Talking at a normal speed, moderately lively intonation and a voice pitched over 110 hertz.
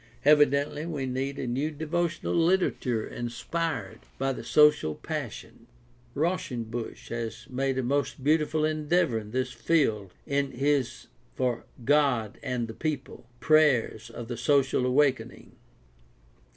No: slow, 125 wpm; average, 3.9 semitones; low, 135 Hz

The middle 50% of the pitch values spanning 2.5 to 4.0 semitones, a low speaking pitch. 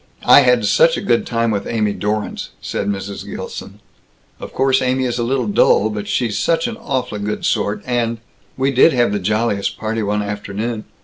Yes: average, 3.3 semitones; low, 115 Hz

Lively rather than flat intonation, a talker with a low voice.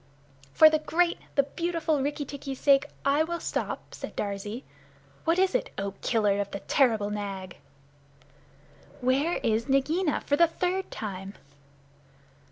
No: wide, 7.6 semitones; very high, 275 Hz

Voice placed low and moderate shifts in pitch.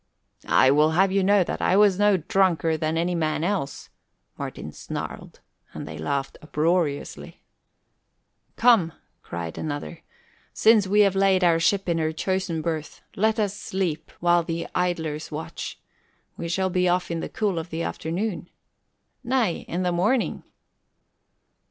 No: medium, 175 Hz; average, 3.3 semitones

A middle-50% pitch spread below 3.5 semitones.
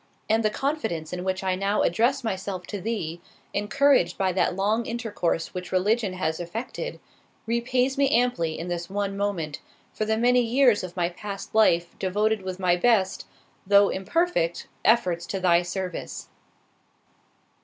No: average, 4.3 semitones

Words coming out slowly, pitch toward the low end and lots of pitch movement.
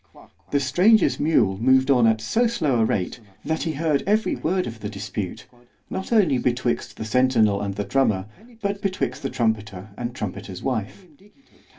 No: average, 170 wpm; low, 125 Hz; wide, 6.7 semitones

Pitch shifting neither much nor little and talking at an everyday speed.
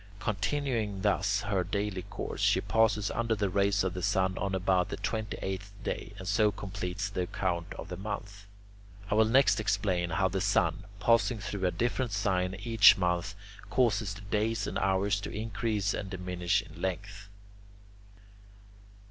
No: narrow, 2.0 semitones; average, 165 wpm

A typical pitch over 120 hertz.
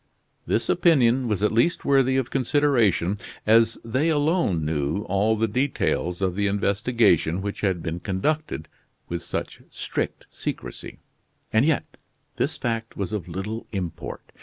No: low, 110 Hz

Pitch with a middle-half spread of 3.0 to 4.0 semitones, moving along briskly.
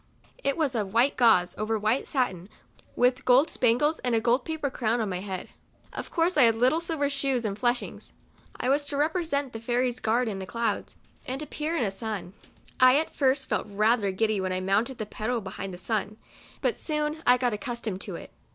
No: average, 4.6 semitones; fast, 210 wpm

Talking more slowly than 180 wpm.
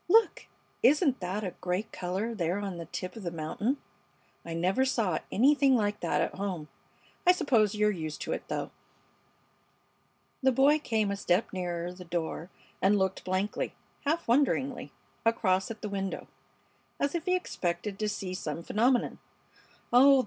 Yes: average, 160 wpm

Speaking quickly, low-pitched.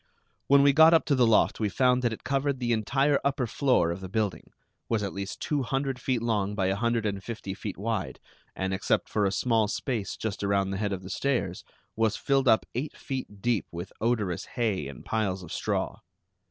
Yes: fast, 215 wpm; low, 110 Hz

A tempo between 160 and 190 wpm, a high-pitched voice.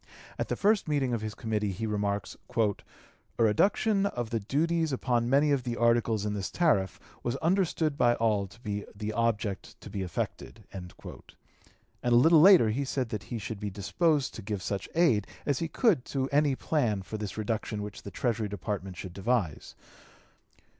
No: average, 180 wpm; low, 115 Hz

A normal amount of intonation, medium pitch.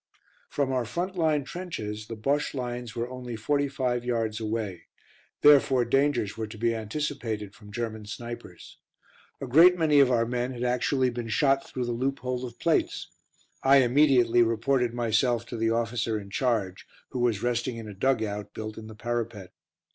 No: average, 3.1 semitones; low, 120 Hz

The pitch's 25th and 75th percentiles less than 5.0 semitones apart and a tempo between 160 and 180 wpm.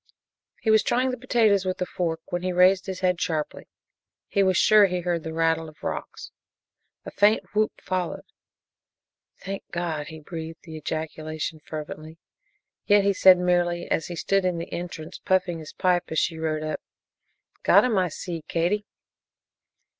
Yes: average, 2.9 semitones; average, 170 wpm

